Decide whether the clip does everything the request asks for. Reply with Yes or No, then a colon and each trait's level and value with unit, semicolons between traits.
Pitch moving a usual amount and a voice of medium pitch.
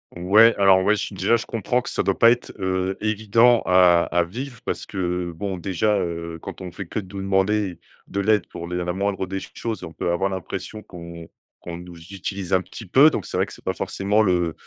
No: average, 3.2 semitones; very low, 95 Hz